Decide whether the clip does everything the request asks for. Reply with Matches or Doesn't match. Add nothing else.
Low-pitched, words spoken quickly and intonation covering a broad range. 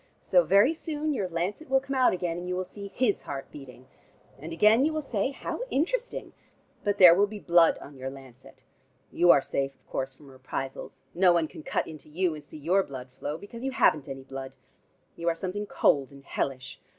Doesn't match